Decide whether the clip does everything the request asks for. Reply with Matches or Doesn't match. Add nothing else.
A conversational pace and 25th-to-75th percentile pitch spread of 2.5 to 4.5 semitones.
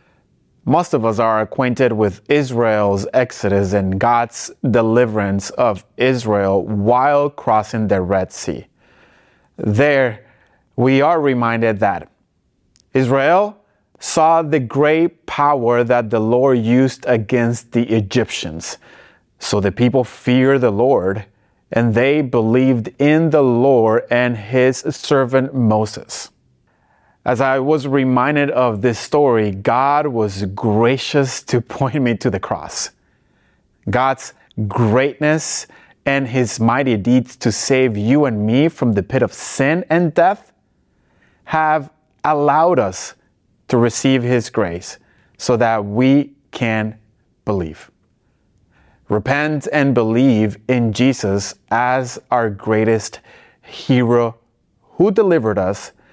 Doesn't match